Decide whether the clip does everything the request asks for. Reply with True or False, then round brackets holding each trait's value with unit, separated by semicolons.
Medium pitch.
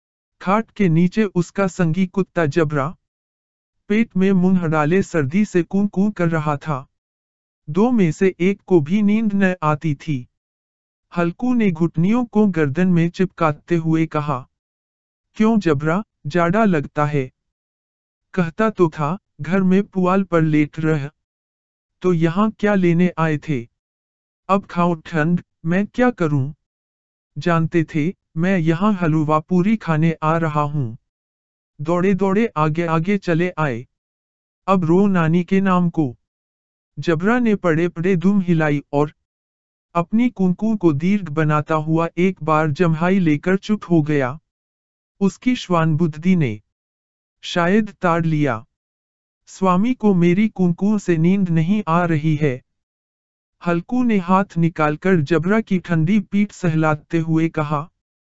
True (165 Hz)